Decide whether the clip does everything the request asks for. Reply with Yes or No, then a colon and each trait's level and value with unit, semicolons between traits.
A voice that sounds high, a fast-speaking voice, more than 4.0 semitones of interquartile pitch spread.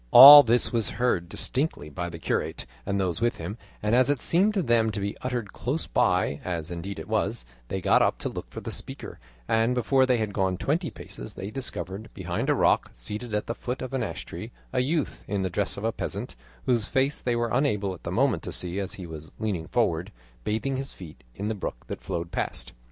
No: low, 110 Hz; fast, 230 wpm; average, 5.2 semitones